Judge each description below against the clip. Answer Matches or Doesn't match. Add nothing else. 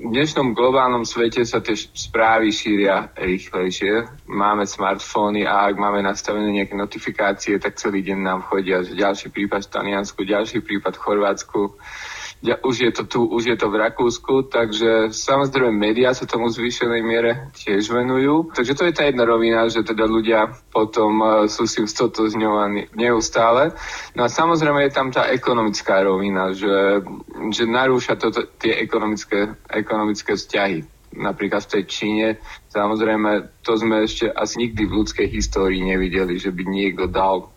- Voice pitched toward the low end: Matches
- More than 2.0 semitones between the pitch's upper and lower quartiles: Matches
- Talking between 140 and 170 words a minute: Matches